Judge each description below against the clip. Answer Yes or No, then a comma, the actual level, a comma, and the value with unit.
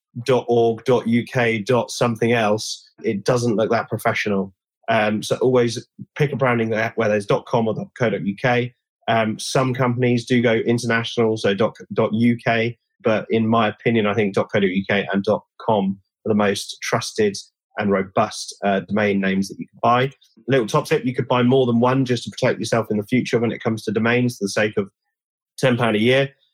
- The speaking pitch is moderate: No, low, 115 Hz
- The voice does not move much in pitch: Yes, narrow, 2.2 semitones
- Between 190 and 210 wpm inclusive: Yes, average, 200 wpm